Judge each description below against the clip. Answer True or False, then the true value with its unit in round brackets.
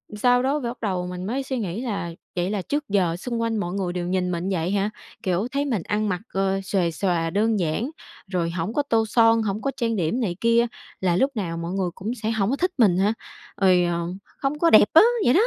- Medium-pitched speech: False (200 Hz)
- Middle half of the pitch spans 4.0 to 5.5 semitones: True (4.5 semitones)